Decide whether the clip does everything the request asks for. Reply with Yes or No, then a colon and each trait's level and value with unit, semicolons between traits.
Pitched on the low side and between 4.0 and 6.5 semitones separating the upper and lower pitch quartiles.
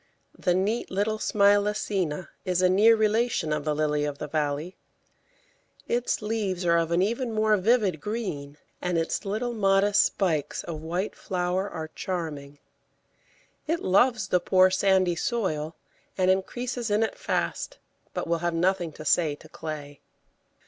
No: medium, 185 Hz; average, 4.6 semitones